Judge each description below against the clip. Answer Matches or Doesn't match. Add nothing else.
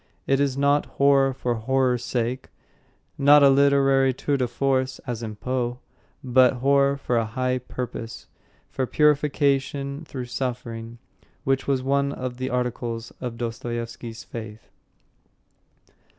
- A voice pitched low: Matches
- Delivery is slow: Matches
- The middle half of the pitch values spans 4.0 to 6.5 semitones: Doesn't match